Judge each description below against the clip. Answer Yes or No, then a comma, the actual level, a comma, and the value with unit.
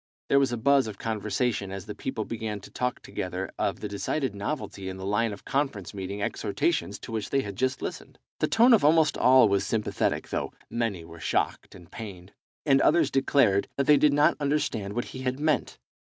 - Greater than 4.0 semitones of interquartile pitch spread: Yes, wide, 5.6 semitones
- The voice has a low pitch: Yes, low, 115 Hz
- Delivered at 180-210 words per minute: Yes, fast, 205 wpm